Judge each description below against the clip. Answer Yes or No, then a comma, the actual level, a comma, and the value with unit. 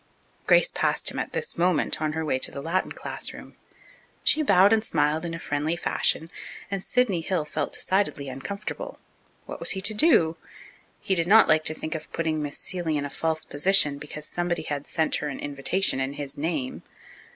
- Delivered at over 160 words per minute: Yes, average, 195 wpm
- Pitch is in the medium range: Yes, medium, 160 Hz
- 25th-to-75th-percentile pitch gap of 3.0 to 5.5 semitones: Yes, average, 4.0 semitones